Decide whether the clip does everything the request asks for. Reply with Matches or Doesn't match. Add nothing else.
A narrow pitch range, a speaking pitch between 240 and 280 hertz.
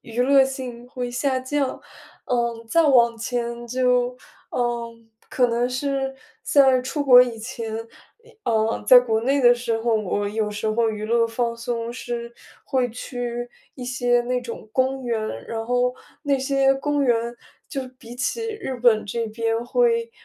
Matches